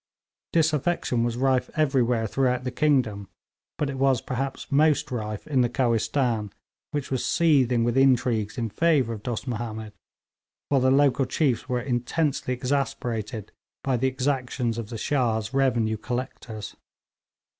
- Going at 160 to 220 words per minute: No, average, 140 wpm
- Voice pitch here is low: Yes, low, 125 Hz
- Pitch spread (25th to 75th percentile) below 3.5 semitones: Yes, average, 2.9 semitones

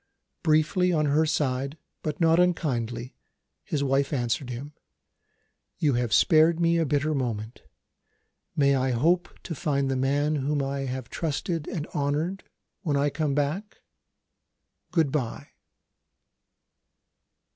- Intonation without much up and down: No, average, 3.0 semitones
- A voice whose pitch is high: No, medium, 145 Hz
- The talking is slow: Yes, slow, 125 wpm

